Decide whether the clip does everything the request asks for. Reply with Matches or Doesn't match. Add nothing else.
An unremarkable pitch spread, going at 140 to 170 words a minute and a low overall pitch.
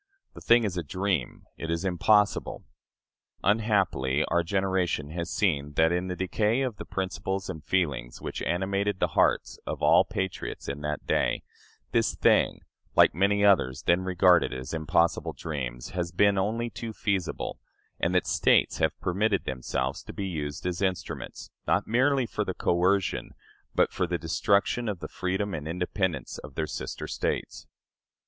Matches